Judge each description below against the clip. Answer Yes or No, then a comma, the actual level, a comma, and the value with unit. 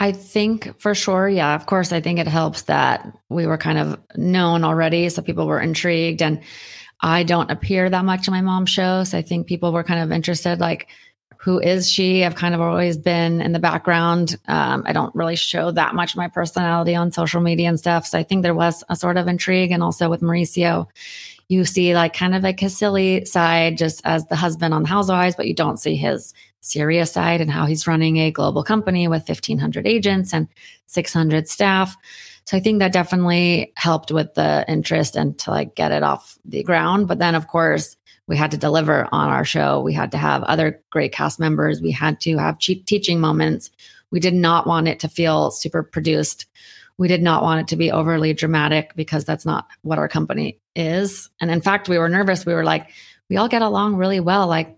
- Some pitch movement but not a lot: No, narrow, 2.3 semitones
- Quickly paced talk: Yes, fast, 220 wpm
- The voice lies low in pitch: No, medium, 170 Hz